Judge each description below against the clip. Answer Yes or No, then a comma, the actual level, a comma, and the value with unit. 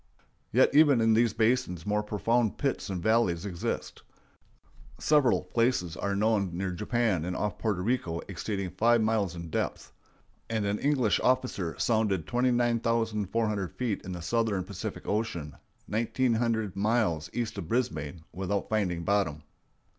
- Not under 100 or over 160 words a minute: Yes, average, 140 wpm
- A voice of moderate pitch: No, low, 105 Hz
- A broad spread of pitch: No, average, 4.2 semitones